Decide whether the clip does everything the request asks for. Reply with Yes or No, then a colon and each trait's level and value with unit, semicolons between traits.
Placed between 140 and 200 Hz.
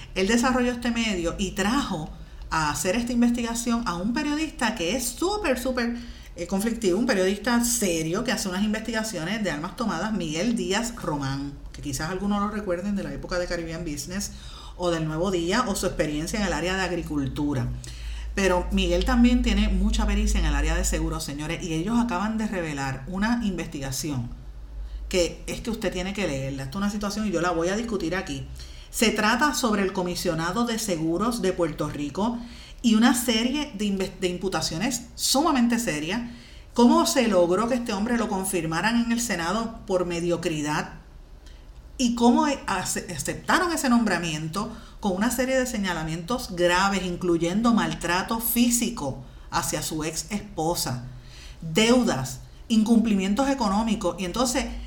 Yes: high, 190 Hz